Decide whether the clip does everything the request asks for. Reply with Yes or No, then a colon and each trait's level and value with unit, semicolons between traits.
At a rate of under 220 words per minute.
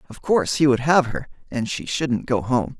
No: fast, 235 wpm